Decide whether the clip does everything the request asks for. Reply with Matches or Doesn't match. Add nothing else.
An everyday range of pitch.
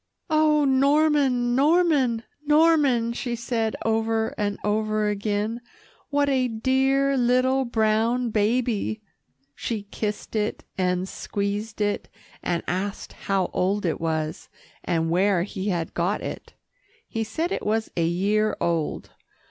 Matches